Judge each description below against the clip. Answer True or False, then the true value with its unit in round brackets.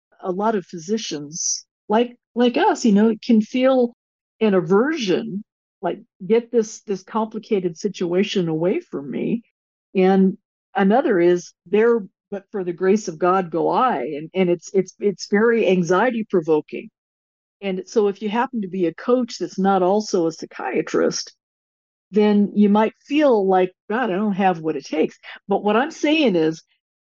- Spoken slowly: False (160 wpm)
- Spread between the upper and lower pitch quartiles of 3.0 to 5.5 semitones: True (3.7 semitones)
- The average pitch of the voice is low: False (200 Hz)